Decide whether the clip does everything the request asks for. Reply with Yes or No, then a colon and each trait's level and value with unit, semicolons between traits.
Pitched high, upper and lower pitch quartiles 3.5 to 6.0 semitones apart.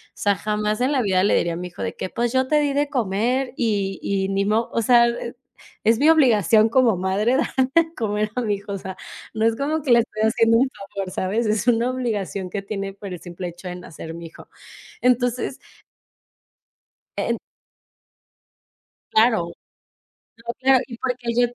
Yes: high, 220 Hz; average, 4.0 semitones